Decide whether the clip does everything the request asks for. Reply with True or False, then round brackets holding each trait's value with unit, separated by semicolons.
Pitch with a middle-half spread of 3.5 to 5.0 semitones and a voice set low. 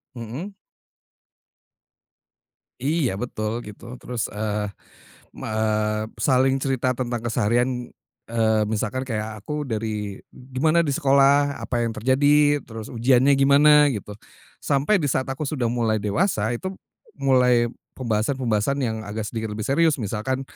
True (4.0 semitones; 125 Hz)